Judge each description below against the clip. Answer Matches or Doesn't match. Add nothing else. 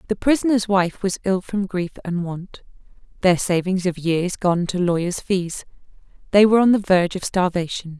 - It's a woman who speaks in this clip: Matches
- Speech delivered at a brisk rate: Doesn't match